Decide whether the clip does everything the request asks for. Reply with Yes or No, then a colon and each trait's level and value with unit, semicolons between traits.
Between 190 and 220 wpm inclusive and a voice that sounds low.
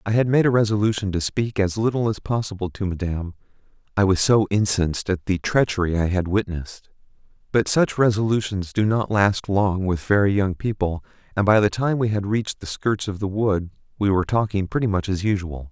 Yes: average, 200 wpm; low, 100 Hz